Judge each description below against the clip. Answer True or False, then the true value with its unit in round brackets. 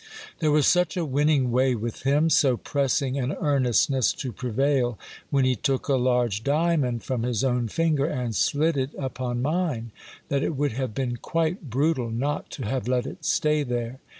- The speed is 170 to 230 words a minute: True (180 wpm)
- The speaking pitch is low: True (130 Hz)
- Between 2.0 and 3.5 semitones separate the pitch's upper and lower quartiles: True (3.1 semitones)